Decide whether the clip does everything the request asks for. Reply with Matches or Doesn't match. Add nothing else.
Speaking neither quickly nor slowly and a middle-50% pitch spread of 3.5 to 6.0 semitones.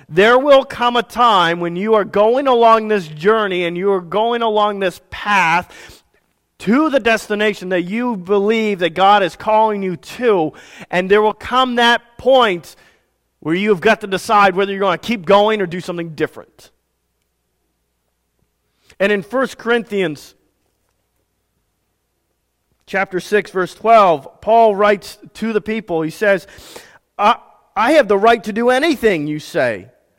Matches